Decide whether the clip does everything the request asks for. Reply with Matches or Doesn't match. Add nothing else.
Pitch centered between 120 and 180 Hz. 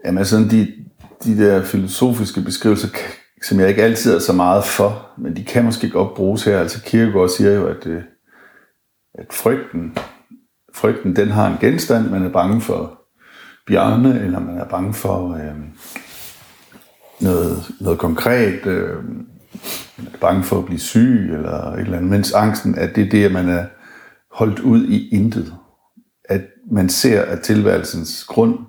Doesn't match